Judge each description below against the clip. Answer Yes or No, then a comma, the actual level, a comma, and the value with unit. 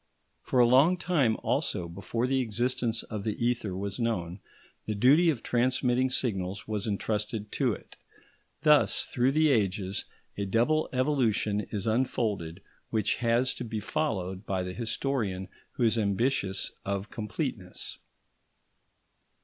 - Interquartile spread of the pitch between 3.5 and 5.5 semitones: Yes, average, 4.3 semitones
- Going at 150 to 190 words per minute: No, slow, 135 wpm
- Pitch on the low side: Yes, low, 110 Hz